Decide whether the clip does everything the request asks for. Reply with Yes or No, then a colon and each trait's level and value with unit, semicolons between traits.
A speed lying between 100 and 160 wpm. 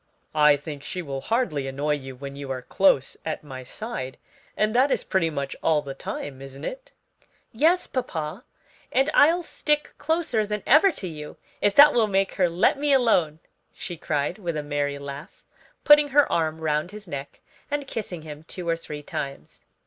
No: average, 185 wpm